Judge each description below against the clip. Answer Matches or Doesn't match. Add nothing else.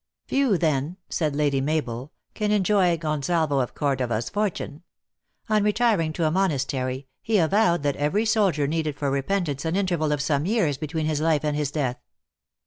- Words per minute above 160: Matches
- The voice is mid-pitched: Matches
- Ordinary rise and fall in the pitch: Matches